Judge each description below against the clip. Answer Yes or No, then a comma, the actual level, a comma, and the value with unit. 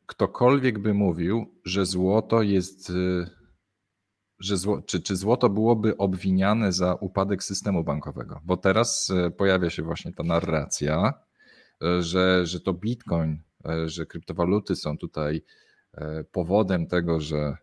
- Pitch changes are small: No, average, 3.3 semitones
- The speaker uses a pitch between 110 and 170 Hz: No, very low, 95 Hz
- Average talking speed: Yes, average, 120 wpm